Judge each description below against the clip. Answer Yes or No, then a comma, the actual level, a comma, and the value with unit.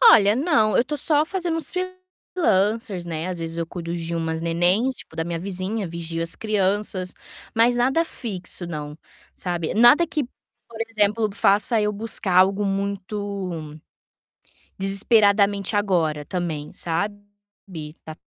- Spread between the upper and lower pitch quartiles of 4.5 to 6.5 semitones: Yes, average, 4.8 semitones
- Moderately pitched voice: No, high, 200 Hz